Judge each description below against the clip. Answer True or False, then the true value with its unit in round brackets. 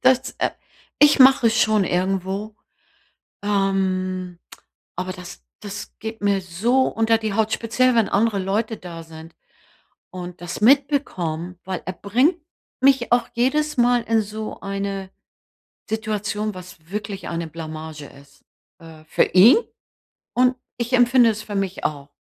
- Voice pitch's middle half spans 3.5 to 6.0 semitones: True (4.1 semitones)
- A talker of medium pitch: False (200 Hz)